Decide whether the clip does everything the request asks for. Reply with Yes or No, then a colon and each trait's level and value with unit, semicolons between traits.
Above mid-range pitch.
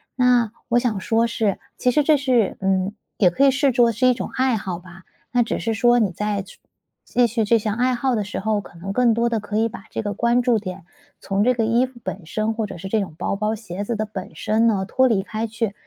Yes: high, 220 Hz